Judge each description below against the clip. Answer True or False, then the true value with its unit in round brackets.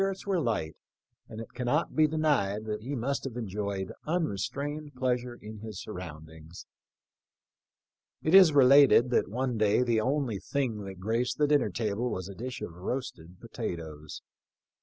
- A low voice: True (120 Hz)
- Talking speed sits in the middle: True (160 wpm)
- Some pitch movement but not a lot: False (6.0 semitones)